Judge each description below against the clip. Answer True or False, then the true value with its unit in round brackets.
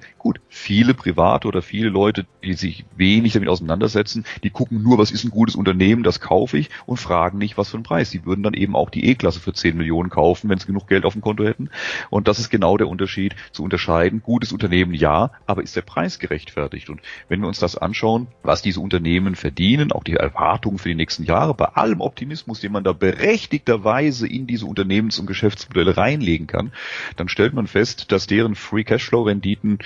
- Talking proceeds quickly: True (210 wpm)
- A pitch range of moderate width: True (3.4 semitones)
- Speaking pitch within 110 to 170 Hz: False (100 Hz)